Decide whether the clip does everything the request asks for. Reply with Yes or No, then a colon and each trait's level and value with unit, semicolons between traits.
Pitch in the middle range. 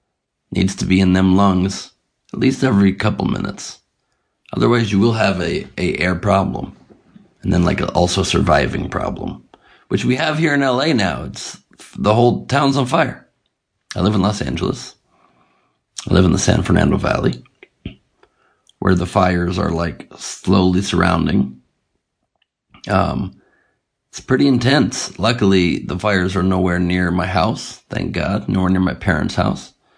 No: very low, 95 Hz